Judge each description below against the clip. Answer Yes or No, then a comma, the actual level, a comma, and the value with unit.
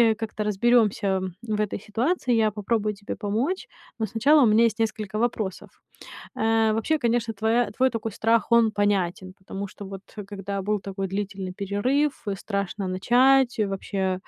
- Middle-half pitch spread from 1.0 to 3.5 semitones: Yes, average, 2.8 semitones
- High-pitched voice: Yes, high, 215 Hz